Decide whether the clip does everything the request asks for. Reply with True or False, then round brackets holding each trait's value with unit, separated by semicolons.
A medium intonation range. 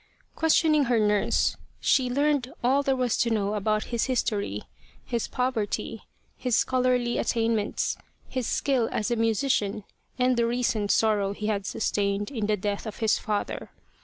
True (3.3 semitones)